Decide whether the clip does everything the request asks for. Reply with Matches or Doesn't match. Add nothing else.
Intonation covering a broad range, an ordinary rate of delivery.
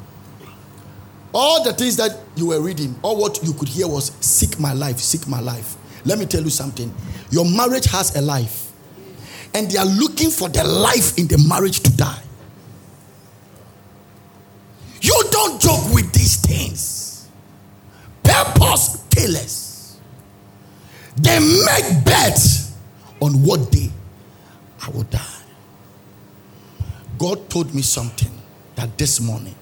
Doesn't match